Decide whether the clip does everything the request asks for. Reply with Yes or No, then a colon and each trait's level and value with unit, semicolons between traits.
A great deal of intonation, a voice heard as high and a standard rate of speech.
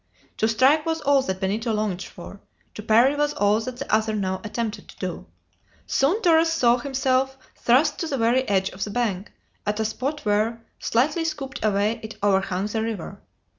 No: average, 4.6 semitones; high, 230 Hz; average, 185 wpm